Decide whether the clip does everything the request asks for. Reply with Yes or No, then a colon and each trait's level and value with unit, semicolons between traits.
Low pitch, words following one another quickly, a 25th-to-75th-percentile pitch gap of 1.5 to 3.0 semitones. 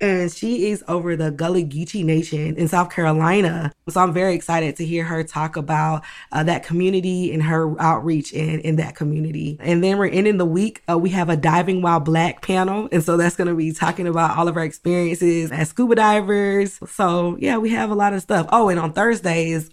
No: medium, 170 Hz; fast, 215 wpm; average, 2.7 semitones